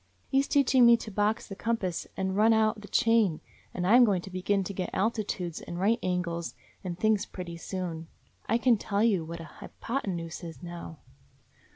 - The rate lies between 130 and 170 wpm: No, average, 195 wpm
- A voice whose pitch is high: Yes, high, 195 Hz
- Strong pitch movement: No, average, 4.2 semitones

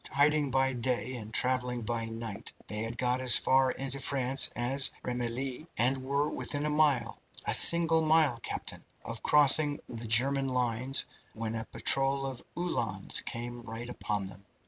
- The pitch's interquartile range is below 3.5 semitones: Yes, average, 2.9 semitones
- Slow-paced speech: No, average, 160 wpm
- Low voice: Yes, low, 125 Hz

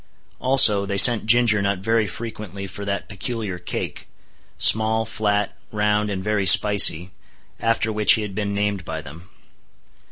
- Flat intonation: Yes, narrow, 2.0 semitones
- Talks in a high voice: No, low, 105 Hz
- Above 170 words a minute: No, slow, 135 wpm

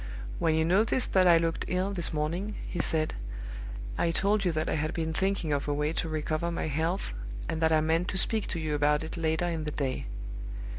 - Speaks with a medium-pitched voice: Yes, medium, 160 Hz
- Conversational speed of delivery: No, fast, 220 wpm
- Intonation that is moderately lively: No, narrow, 2.3 semitones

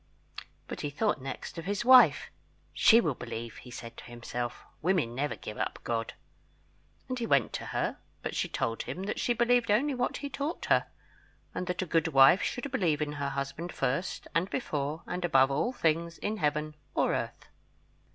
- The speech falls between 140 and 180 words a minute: No, average, 190 wpm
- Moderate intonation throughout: No, wide, 7.7 semitones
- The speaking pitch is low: No, medium, 165 Hz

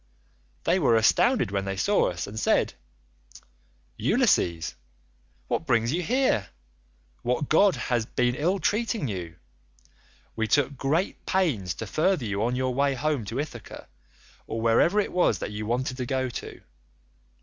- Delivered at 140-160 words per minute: Yes, average, 150 wpm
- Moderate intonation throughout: No, wide, 6.6 semitones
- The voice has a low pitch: Yes, low, 125 Hz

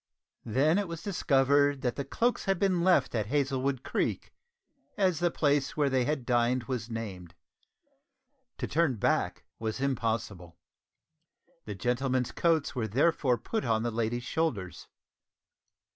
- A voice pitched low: Yes, low, 130 Hz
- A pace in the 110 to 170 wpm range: Yes, average, 140 wpm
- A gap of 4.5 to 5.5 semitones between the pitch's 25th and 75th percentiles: Yes, average, 5.1 semitones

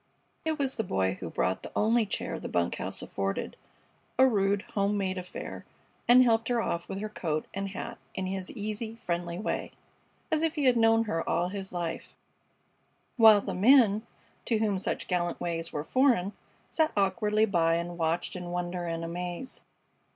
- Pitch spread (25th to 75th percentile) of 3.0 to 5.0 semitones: Yes, average, 4.5 semitones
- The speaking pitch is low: No, high, 195 Hz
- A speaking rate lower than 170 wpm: No, average, 180 wpm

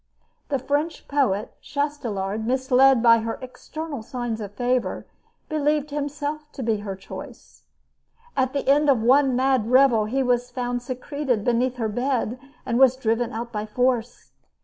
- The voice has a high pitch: Yes, very high, 250 Hz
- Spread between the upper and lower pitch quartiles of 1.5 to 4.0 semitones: Yes, average, 3.1 semitones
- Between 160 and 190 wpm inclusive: No, average, 150 wpm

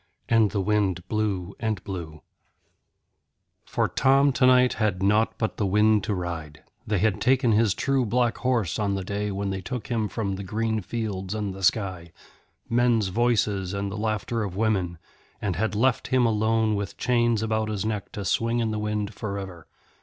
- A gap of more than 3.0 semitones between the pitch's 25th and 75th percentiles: No, average, 2.7 semitones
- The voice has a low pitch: Yes, low, 105 Hz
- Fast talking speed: No, average, 185 wpm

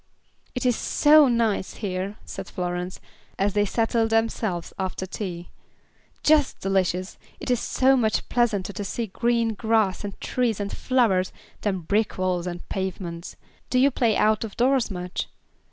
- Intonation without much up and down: No, average, 4.0 semitones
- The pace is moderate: Yes, average, 155 wpm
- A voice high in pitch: Yes, high, 205 Hz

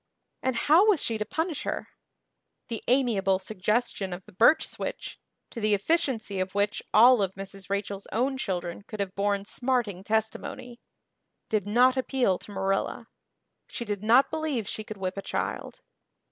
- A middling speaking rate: Yes, average, 160 wpm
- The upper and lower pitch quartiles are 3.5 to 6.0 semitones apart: Yes, average, 4.3 semitones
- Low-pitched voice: No, high, 215 Hz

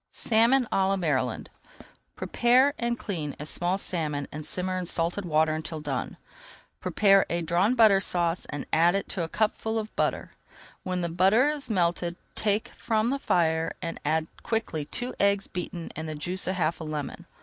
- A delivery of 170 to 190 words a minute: Yes, average, 180 wpm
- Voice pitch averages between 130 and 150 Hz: No, medium, 180 Hz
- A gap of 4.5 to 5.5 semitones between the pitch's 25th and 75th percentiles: Yes, average, 4.8 semitones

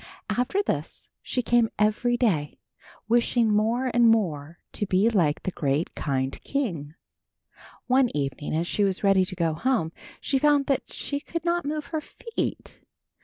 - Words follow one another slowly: No, average, 160 wpm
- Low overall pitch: No, high, 220 Hz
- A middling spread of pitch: No, wide, 7.8 semitones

